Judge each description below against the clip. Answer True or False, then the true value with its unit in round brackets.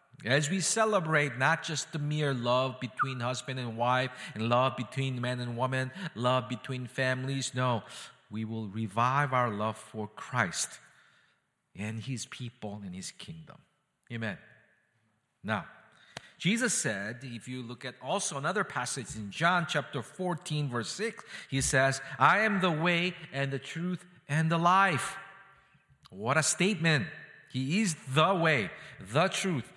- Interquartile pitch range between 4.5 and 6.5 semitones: True (4.8 semitones)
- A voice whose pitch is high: False (135 Hz)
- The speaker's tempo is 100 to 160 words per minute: True (145 wpm)